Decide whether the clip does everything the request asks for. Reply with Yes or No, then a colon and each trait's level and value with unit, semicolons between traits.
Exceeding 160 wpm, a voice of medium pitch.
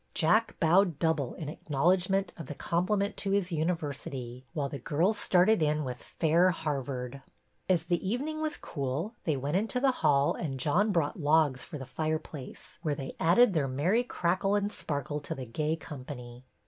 Yes: average, 175 wpm; medium, 160 Hz